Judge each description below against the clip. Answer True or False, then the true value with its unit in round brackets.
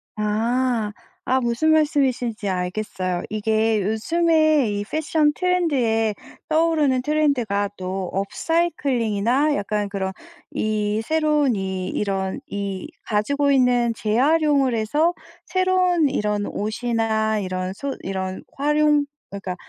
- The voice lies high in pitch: True (230 Hz)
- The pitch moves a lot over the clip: True (6.4 semitones)